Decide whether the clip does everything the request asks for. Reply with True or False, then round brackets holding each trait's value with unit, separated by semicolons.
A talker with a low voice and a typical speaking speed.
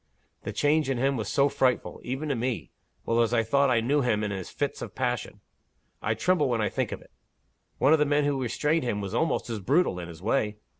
False (130 Hz; 245 wpm)